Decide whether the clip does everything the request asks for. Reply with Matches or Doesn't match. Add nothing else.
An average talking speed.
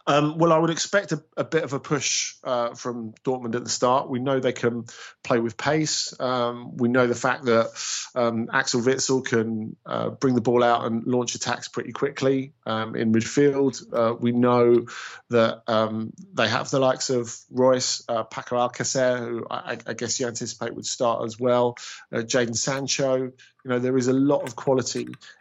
Matches